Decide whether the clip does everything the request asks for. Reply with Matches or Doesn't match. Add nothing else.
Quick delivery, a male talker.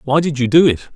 Matches